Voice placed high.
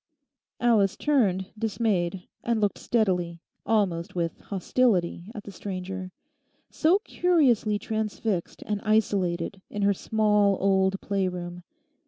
Yes: high, 200 Hz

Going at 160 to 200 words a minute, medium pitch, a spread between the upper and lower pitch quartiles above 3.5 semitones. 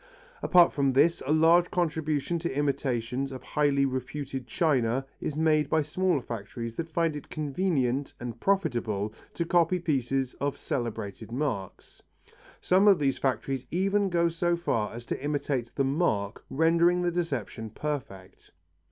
No: average, 145 wpm; medium, 145 Hz; average, 5.2 semitones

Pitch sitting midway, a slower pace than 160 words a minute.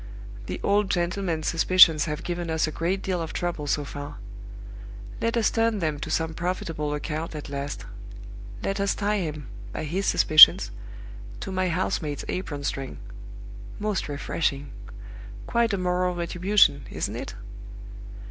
Yes: medium, 170 Hz; average, 150 wpm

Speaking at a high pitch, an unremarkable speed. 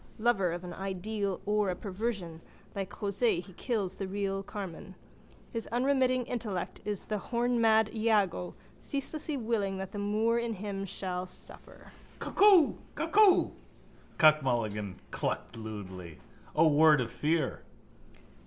No: high, 200 Hz; slow, 130 wpm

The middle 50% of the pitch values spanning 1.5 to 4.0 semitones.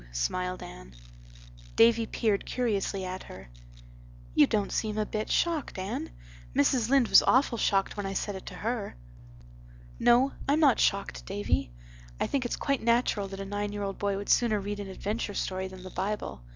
Yes: average, 3.3 semitones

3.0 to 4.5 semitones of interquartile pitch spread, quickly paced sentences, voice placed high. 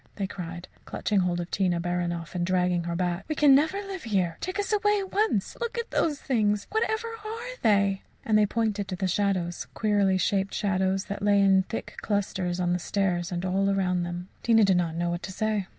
Yes: average, 3.8 semitones; fast, 215 wpm; high, 195 Hz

